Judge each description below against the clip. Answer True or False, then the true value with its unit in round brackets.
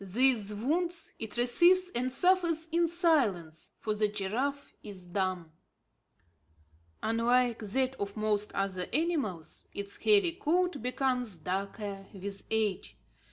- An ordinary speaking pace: False (115 wpm)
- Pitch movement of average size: False (7.6 semitones)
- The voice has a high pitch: True (230 Hz)